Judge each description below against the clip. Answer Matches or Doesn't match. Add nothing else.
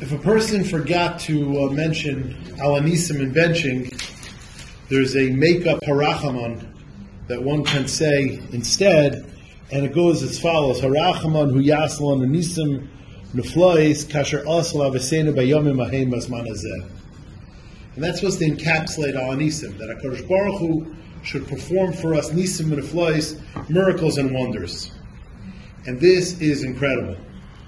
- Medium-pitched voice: Matches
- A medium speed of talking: Doesn't match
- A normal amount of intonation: Matches